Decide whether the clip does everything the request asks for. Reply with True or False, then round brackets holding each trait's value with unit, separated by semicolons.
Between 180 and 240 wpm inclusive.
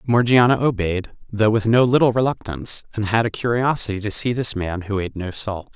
True (200 wpm)